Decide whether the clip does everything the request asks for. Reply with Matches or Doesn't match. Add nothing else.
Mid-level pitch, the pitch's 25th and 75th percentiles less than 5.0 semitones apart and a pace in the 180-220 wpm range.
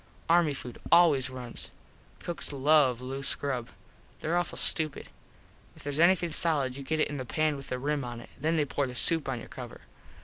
Matches